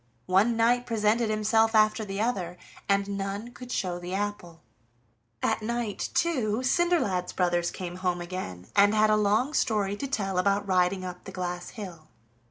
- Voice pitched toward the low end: No, high, 200 Hz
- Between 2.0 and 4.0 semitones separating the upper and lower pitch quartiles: Yes, average, 3.4 semitones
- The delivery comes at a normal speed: Yes, average, 165 wpm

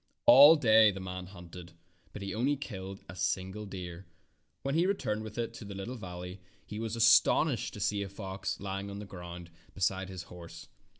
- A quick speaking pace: No, average, 190 wpm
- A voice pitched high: No, low, 100 Hz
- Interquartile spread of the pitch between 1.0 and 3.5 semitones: Yes, average, 3.0 semitones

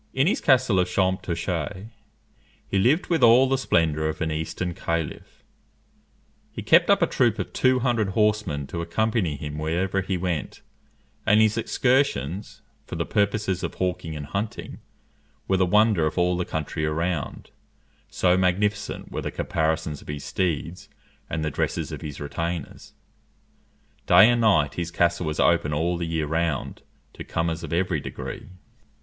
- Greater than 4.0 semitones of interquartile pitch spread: Yes, average, 4.6 semitones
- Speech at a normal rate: Yes, average, 160 wpm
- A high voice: No, very low, 90 Hz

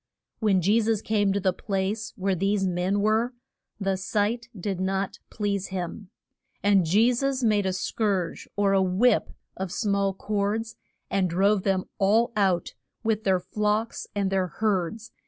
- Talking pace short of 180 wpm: Yes, average, 155 wpm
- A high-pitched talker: Yes, high, 200 Hz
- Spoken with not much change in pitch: Yes, narrow, 2.3 semitones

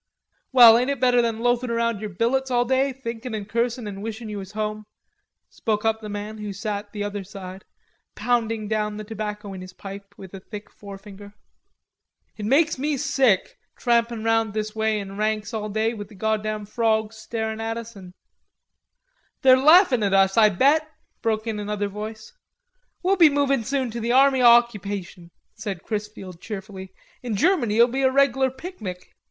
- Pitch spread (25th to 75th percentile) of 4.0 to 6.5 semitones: No, average, 2.8 semitones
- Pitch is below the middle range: No, high, 220 Hz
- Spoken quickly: No, average, 180 wpm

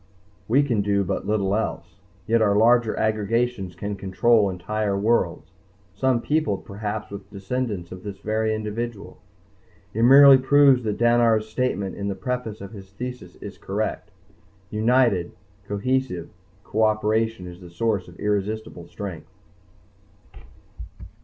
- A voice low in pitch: Yes, low, 110 Hz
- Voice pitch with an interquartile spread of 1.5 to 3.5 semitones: Yes, average, 3.1 semitones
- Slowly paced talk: Yes, slow, 130 wpm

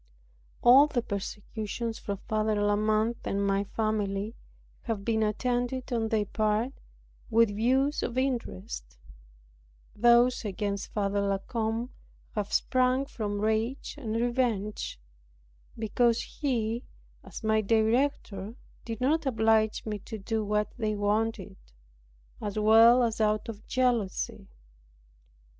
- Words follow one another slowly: Yes, slow, 120 wpm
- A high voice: Yes, high, 220 Hz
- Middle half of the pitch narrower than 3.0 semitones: Yes, narrow, 2.5 semitones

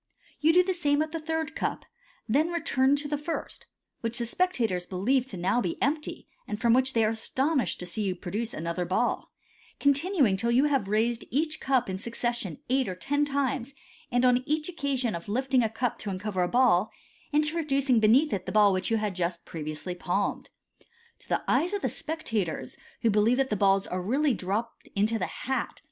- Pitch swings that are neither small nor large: No, wide, 6.2 semitones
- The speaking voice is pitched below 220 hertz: No, high, 240 Hz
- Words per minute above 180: Yes, average, 200 wpm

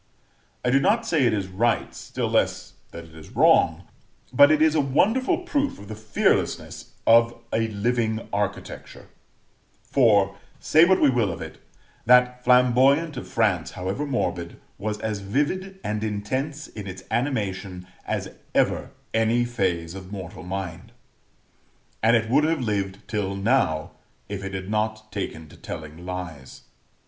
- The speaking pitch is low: Yes, low, 110 Hz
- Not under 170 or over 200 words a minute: No, average, 155 wpm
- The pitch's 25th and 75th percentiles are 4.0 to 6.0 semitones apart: Yes, wide, 5.4 semitones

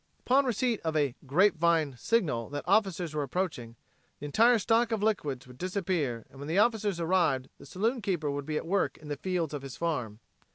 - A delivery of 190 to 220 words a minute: Yes, average, 195 wpm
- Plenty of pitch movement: Yes, wide, 6.0 semitones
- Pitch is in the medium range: Yes, medium, 170 Hz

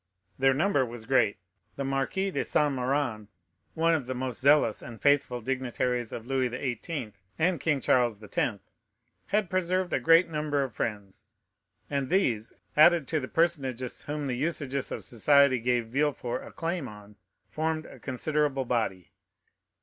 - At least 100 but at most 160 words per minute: Yes, average, 155 wpm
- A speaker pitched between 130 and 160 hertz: Yes, low, 135 Hz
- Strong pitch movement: No, average, 4.0 semitones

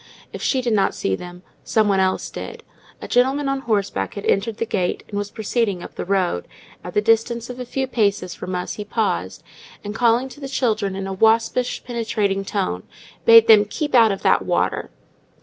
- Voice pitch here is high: Yes, high, 215 Hz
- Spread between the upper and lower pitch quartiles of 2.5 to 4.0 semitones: Yes, average, 3.6 semitones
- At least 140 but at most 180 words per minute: No, average, 200 wpm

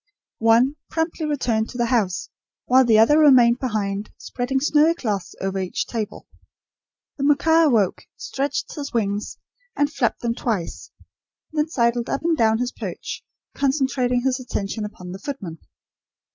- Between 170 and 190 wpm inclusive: No, average, 145 wpm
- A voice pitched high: Yes, high, 245 Hz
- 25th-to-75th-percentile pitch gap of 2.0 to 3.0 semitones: No, average, 4.5 semitones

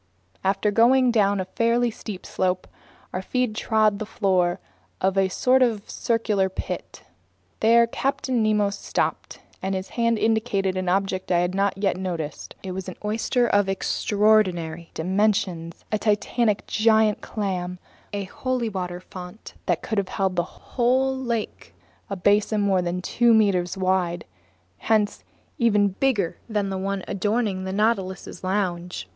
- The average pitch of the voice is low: No, high, 200 Hz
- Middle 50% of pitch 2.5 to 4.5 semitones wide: Yes, average, 2.9 semitones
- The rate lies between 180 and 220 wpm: No, average, 150 wpm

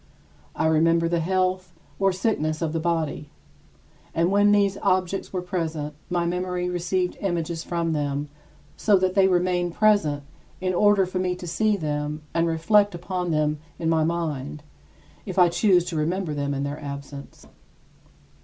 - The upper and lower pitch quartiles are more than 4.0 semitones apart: No, average, 2.9 semitones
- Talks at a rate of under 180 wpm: Yes, average, 160 wpm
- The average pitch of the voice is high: No, medium, 170 Hz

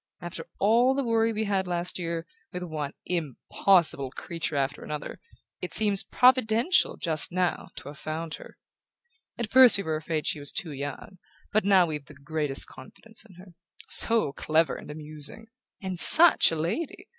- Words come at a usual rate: Yes, average, 170 wpm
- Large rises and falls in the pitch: Yes, wide, 5.9 semitones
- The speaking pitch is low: No, medium, 175 Hz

